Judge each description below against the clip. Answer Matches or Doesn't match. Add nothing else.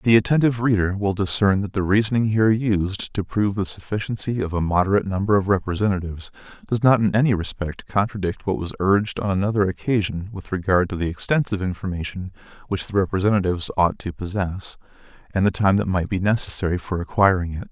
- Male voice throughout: Matches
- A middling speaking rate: Matches